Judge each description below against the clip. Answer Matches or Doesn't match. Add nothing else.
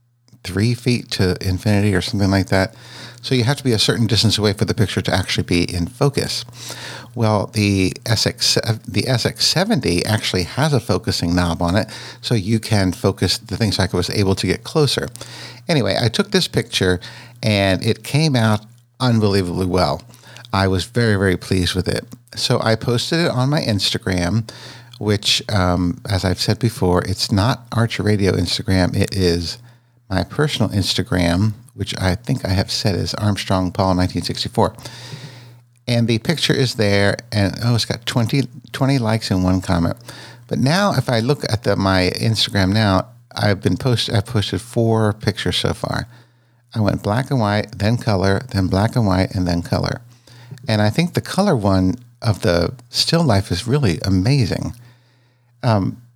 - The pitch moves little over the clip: Doesn't match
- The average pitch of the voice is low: Matches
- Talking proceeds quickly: Doesn't match